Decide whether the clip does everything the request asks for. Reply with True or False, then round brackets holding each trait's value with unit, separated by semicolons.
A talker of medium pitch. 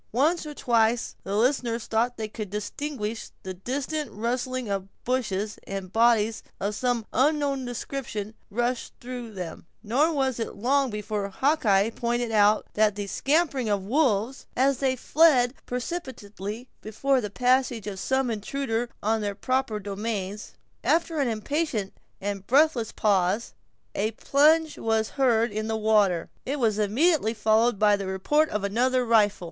False (230 Hz)